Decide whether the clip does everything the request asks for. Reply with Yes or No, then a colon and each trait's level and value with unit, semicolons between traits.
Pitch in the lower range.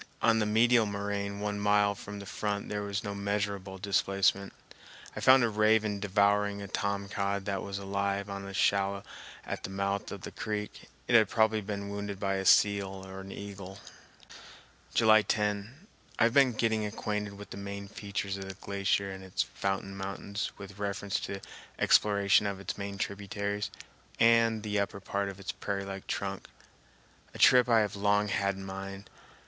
Yes: low, 100 Hz